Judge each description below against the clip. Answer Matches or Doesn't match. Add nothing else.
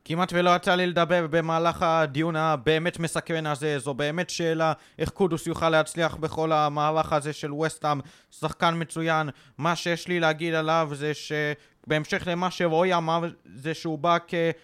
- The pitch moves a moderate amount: Doesn't match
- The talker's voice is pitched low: Doesn't match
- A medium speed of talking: Doesn't match